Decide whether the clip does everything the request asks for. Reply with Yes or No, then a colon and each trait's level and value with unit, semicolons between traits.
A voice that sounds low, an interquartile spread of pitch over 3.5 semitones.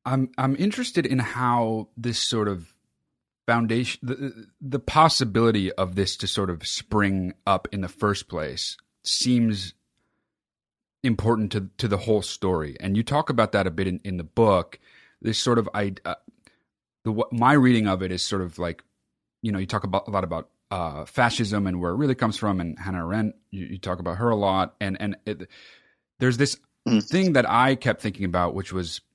Yes: low, 105 Hz; average, 4.0 semitones